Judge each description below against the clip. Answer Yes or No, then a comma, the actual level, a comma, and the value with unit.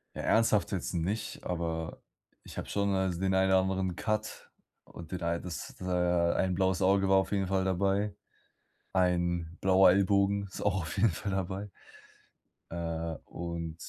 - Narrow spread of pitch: Yes, narrow, 2.3 semitones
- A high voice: No, very low, 95 Hz